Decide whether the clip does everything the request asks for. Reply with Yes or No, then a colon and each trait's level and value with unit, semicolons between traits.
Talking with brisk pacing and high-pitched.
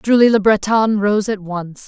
No: average, 190 wpm; high, 210 Hz